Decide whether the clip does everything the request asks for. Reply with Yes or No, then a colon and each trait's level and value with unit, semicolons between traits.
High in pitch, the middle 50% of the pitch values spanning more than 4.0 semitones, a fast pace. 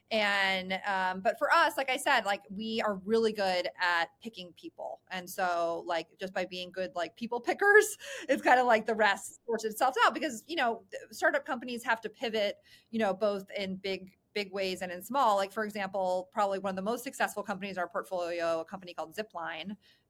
Yes: high, 205 Hz; average, 4.4 semitones; fast, 210 wpm